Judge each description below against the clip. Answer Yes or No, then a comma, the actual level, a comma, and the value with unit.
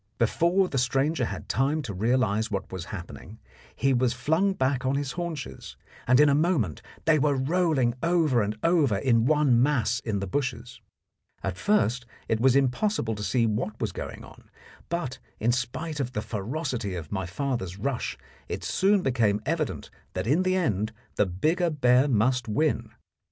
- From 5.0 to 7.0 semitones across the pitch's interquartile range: Yes, wide, 5.6 semitones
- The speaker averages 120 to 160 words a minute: No, average, 170 wpm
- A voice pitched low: Yes, low, 130 Hz